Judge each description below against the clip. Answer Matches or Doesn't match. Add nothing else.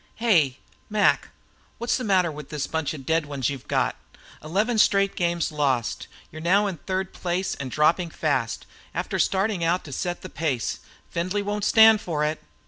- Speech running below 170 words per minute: Doesn't match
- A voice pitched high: Doesn't match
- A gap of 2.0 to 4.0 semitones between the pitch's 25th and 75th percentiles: Doesn't match